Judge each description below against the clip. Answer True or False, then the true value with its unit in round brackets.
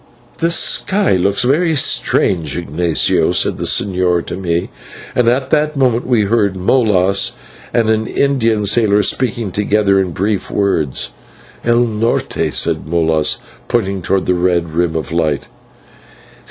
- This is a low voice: True (100 Hz)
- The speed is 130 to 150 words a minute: True (140 wpm)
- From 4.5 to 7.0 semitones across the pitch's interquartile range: True (5.1 semitones)